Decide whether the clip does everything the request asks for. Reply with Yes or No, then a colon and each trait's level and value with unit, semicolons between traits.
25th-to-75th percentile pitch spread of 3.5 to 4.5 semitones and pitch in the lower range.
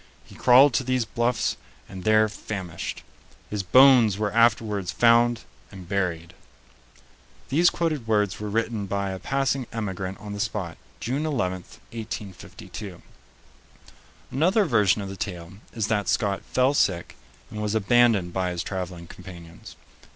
Yes: average, 3.9 semitones; low, 105 Hz